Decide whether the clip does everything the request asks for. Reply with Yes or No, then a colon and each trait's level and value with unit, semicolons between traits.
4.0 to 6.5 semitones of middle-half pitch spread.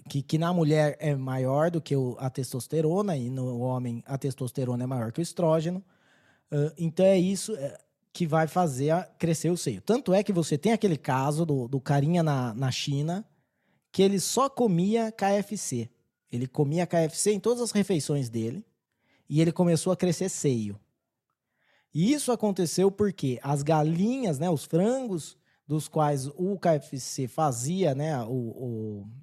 Yes: average, 5.2 semitones